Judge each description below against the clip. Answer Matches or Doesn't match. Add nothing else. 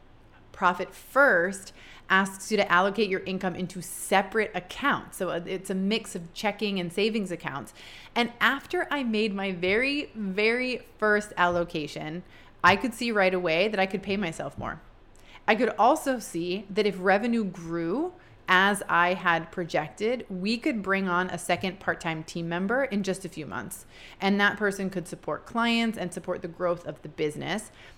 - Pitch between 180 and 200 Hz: Matches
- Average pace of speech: Matches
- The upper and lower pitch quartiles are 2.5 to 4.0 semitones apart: Matches